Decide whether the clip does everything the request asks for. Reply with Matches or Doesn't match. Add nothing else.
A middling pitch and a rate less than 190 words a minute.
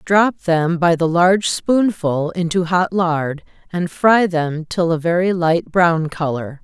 Matches